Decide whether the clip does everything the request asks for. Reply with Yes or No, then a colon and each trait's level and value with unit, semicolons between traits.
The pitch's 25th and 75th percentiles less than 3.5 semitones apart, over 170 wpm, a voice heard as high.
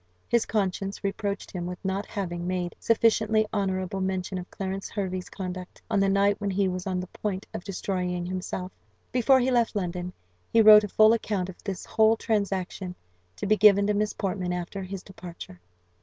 Yes: narrow, 2.4 semitones; average, 185 wpm; high, 195 Hz